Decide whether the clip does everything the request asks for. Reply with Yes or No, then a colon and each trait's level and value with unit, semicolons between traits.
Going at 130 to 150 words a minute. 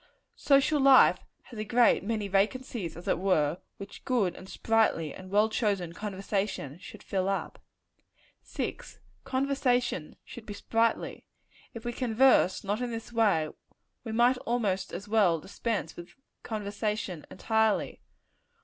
Yes: slow, 135 wpm